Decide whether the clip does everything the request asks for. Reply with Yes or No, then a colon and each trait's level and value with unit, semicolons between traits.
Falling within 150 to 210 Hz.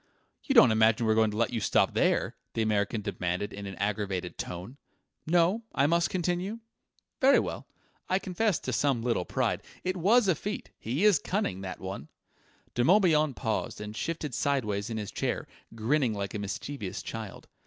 No: low, 115 Hz